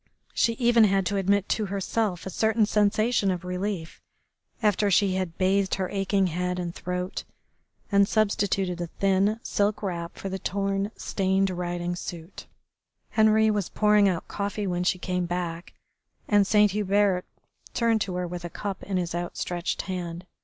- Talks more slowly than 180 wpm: Yes, average, 160 wpm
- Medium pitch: No, high, 195 Hz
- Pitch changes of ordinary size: No, narrow, 2.3 semitones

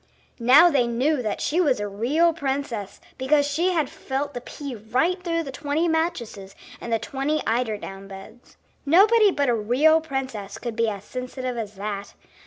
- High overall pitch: Yes, very high, 260 Hz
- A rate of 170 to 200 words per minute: Yes, average, 180 wpm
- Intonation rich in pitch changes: Yes, wide, 5.7 semitones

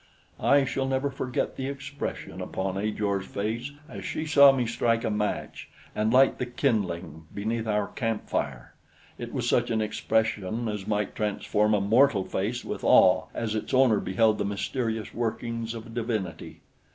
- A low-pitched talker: Yes, low, 110 Hz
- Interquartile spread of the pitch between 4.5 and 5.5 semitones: No, average, 2.9 semitones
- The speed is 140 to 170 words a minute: Yes, average, 165 wpm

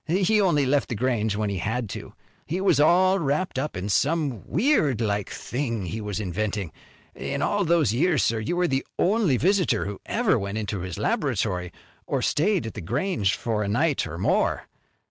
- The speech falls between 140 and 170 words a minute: No, average, 190 wpm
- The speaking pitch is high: No, low, 130 Hz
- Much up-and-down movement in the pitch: Yes, wide, 8.3 semitones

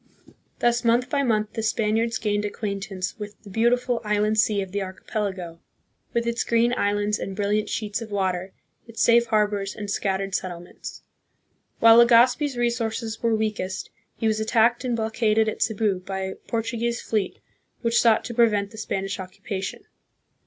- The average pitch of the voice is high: Yes, high, 215 Hz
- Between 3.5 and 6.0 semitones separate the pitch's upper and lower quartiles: No, narrow, 2.5 semitones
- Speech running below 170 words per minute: Yes, average, 160 wpm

